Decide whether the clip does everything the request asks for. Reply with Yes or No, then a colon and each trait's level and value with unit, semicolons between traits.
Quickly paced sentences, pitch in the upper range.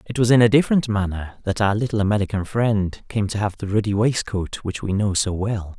No: fast, 230 wpm; low, 105 Hz